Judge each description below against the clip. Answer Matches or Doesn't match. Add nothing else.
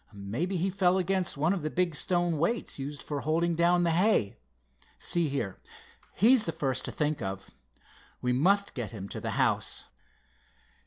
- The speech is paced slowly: Doesn't match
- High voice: Doesn't match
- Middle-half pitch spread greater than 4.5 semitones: Matches